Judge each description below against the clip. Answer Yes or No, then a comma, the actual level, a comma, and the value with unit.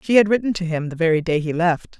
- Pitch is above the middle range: No, medium, 175 Hz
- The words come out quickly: Yes, fast, 300 wpm